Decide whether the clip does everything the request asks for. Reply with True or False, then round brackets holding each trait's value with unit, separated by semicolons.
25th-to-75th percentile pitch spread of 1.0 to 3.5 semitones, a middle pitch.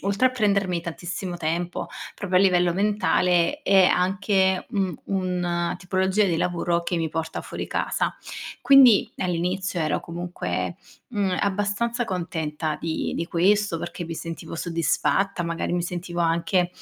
True (2.5 semitones; 180 Hz)